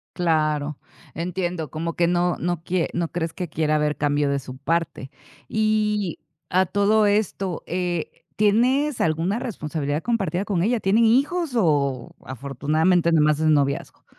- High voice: No, medium, 170 Hz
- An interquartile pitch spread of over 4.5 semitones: Yes, average, 5.0 semitones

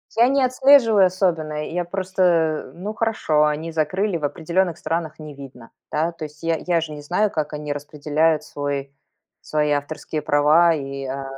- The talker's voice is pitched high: No, medium, 160 Hz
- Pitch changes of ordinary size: Yes, average, 3.3 semitones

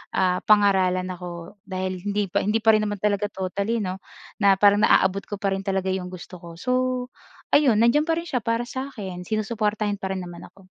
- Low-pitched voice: No, high, 200 Hz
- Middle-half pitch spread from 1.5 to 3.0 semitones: Yes, narrow, 2.4 semitones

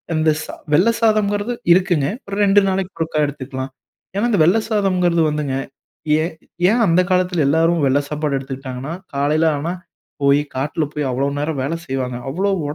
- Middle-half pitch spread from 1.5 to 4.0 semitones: No, average, 5.1 semitones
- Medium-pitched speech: Yes, medium, 160 Hz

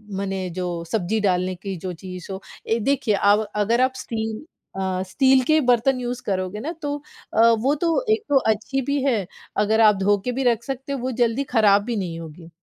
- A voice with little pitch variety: No, average, 5.2 semitones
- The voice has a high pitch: Yes, high, 220 Hz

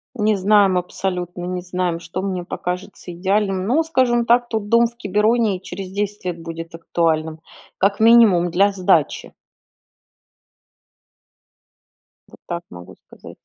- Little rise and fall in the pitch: No, average, 3.1 semitones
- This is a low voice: No, high, 190 Hz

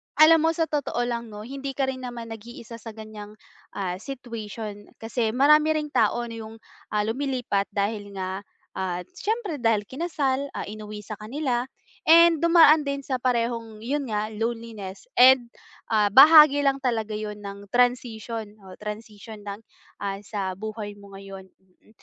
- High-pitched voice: Yes, high, 230 Hz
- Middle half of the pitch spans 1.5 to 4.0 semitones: No, average, 4.4 semitones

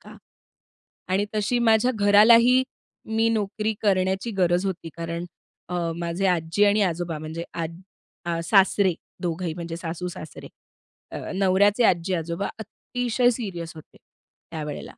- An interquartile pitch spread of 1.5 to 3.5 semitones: No, average, 4.0 semitones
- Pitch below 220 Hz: Yes, medium, 185 Hz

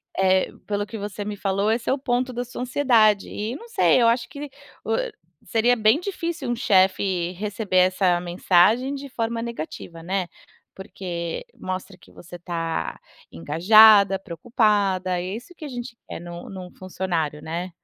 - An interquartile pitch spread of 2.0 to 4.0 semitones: No, average, 4.7 semitones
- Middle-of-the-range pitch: No, high, 205 Hz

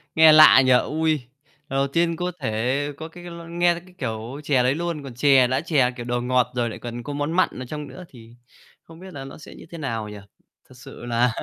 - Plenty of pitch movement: No, average, 4.6 semitones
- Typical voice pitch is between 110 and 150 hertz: Yes, medium, 140 Hz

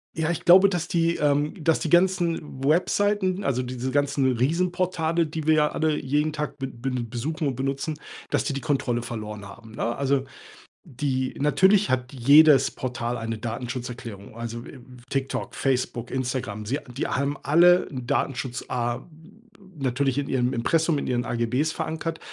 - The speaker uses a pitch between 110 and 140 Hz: Yes, low, 135 Hz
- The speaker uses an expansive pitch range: No, average, 4.4 semitones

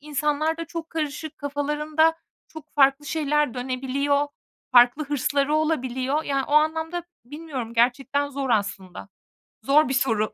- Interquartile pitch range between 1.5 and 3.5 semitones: Yes, average, 2.8 semitones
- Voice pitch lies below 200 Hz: No, very high, 285 Hz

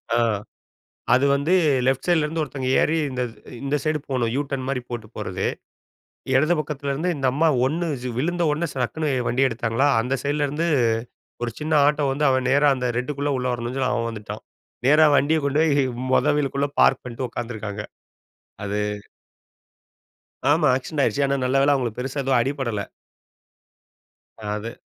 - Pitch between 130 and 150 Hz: Yes, low, 135 Hz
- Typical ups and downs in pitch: Yes, average, 3.1 semitones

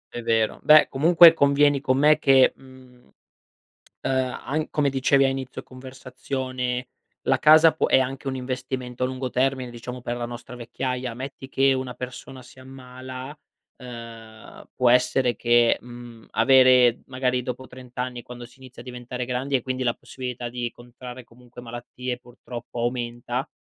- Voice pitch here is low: Yes, low, 125 Hz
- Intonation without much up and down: Yes, narrow, 1.4 semitones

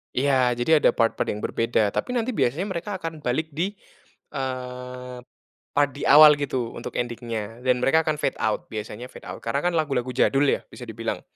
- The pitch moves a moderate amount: Yes, average, 4.1 semitones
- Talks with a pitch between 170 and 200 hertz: No, low, 130 Hz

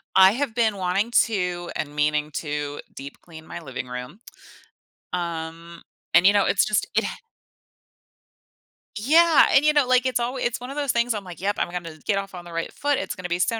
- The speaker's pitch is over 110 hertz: Yes, medium, 185 Hz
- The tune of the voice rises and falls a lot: Yes, wide, 6.2 semitones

